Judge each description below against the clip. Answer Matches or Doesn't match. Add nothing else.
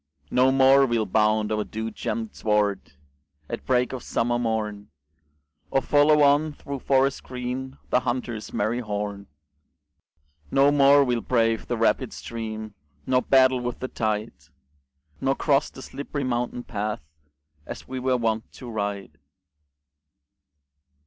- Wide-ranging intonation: Doesn't match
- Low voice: Matches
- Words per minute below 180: Matches